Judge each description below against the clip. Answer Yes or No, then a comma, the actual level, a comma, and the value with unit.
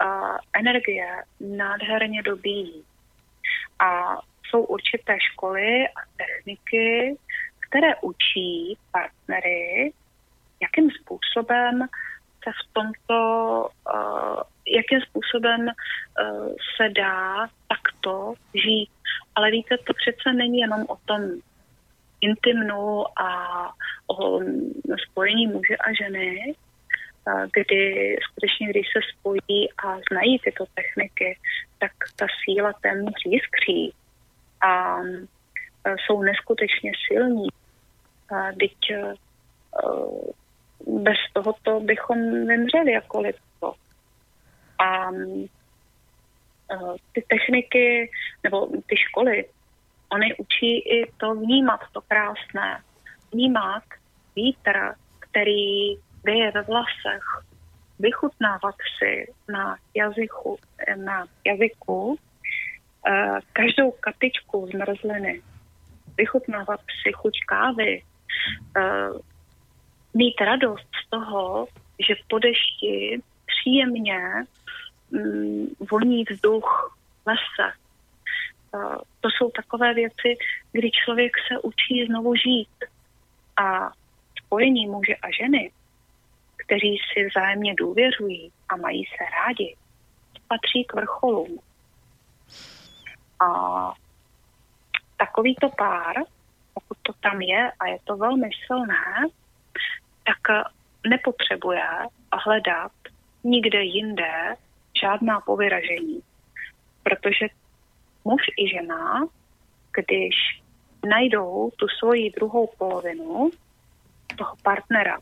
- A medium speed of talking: No, slow, 90 wpm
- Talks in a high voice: Yes, high, 220 Hz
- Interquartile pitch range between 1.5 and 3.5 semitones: No, average, 4.1 semitones